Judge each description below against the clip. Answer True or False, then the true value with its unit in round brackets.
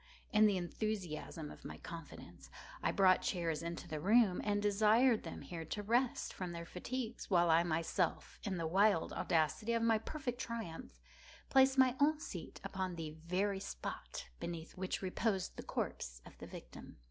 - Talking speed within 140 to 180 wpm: True (170 wpm)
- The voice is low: False (190 Hz)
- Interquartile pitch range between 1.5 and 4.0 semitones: False (4.9 semitones)